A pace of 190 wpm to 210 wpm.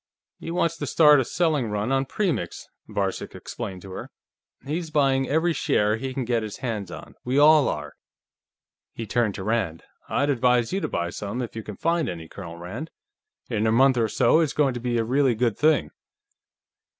Yes: average, 200 wpm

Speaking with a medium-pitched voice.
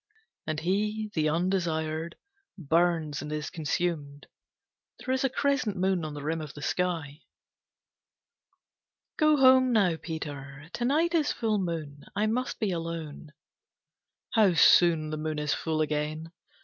Yes: medium, 165 Hz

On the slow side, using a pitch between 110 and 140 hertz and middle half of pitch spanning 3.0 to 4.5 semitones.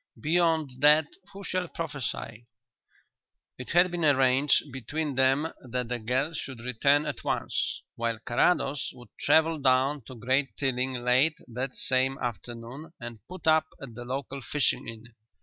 No: average, 150 wpm; low, 135 Hz; average, 3.6 semitones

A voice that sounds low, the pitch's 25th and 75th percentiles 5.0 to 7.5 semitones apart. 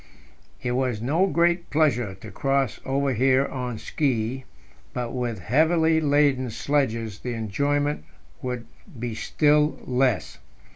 No: low, 130 Hz; average, 3.6 semitones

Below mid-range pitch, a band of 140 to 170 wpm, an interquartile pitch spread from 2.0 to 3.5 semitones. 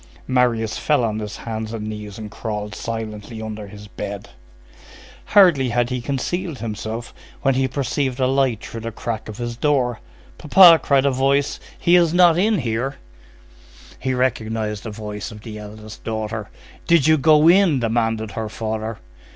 No: low, 115 Hz; average, 165 wpm; average, 4.0 semitones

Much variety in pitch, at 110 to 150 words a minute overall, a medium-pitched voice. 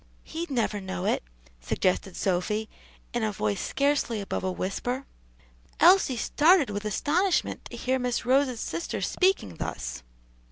No: wide, 6.9 semitones; slow, 135 wpm; high, 230 Hz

